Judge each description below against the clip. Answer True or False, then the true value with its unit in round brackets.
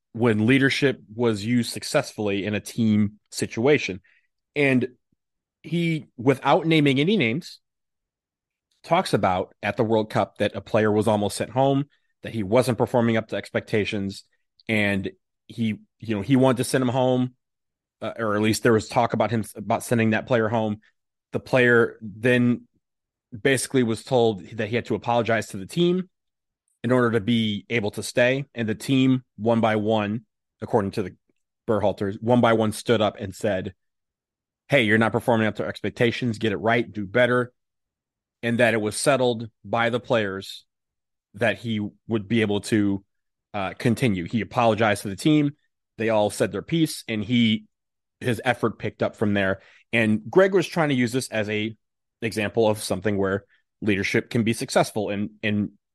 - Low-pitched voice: True (115 Hz)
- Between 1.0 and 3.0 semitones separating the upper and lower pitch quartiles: True (2.7 semitones)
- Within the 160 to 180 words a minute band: True (175 wpm)